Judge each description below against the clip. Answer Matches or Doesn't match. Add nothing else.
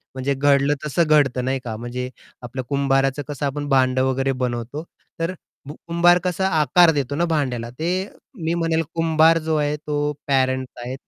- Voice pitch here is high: Doesn't match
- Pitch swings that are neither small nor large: Matches